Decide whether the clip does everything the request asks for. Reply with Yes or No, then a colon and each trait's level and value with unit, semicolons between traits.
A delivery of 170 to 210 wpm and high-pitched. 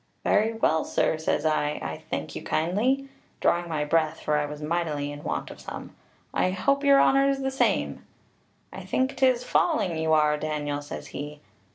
No: average, 180 wpm; medium, 160 Hz